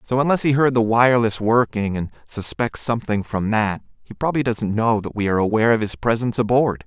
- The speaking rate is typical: No, fast, 210 wpm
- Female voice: No, male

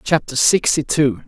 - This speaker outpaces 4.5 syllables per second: No, 4.4 syllables/s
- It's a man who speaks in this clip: Yes, male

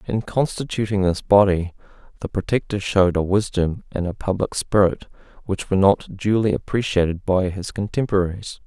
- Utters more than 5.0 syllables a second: Yes, 5.3 syllables/s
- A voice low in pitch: Yes, low, 100 Hz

